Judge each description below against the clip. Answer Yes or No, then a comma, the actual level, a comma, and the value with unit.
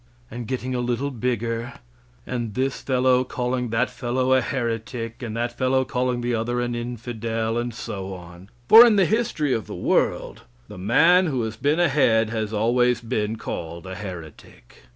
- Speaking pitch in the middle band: No, low, 120 Hz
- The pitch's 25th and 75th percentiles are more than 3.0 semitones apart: No, narrow, 2.4 semitones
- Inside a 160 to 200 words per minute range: Yes, average, 175 wpm